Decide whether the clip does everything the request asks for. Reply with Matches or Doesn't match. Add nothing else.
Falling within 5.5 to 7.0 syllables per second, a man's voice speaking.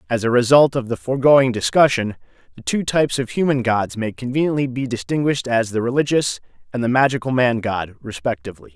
Matches